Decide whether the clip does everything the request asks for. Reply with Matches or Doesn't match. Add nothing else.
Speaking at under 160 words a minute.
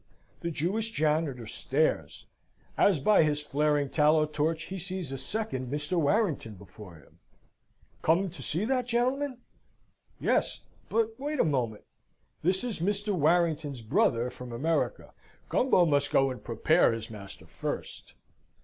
Matches